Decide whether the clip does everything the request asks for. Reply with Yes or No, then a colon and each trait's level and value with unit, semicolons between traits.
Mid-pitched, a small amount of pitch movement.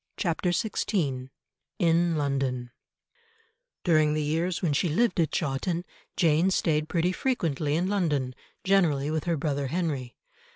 No: medium, 160 Hz; average, 3.6 semitones